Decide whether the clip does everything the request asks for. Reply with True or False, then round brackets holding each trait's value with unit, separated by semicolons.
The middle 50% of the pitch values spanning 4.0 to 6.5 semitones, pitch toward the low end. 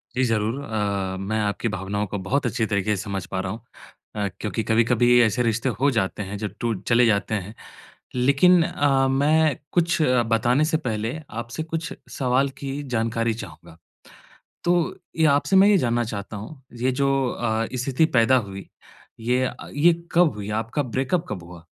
True (4.6 semitones; 115 Hz)